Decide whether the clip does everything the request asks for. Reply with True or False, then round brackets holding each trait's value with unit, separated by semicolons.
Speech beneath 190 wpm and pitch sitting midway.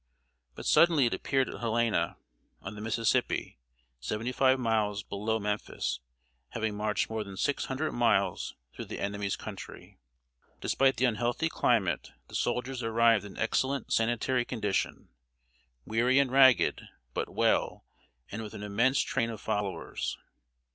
False (140 wpm; 115 Hz)